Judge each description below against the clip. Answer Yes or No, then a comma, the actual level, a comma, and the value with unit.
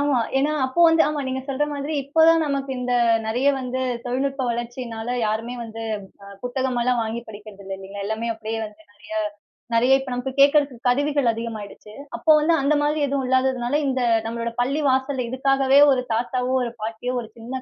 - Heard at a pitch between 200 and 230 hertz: No, very high, 250 Hz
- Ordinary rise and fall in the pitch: Yes, average, 3.1 semitones